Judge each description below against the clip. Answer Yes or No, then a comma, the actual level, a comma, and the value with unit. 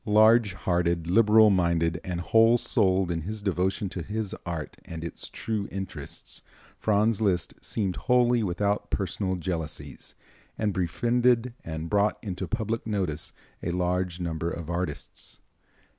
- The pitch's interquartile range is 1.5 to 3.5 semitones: No, average, 4.0 semitones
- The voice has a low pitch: Yes, very low, 95 Hz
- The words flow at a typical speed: No, slow, 130 wpm